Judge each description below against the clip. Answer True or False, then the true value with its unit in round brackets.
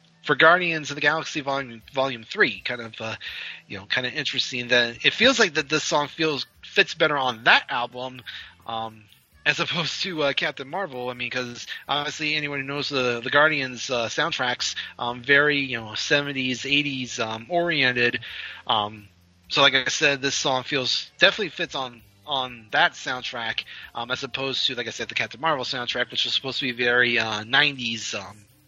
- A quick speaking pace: False (185 wpm)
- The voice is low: True (130 Hz)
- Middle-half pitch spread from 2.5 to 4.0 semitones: True (3.3 semitones)